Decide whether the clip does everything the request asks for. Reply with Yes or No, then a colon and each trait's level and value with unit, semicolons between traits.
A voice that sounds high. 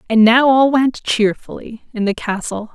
Yes: high, 235 Hz